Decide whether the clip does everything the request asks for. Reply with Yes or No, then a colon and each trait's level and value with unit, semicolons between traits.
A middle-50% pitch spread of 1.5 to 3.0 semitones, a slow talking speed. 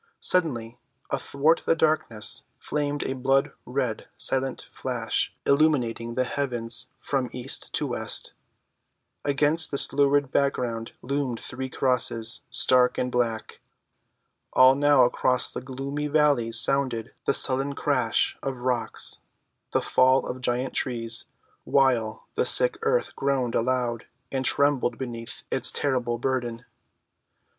Yes: average, 2.7 semitones; slow, 120 wpm